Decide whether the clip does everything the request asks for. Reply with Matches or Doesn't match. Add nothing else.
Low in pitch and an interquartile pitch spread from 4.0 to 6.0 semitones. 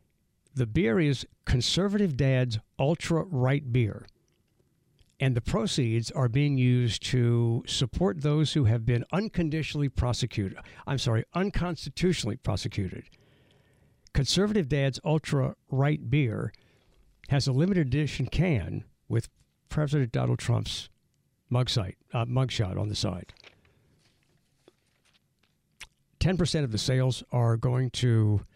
Matches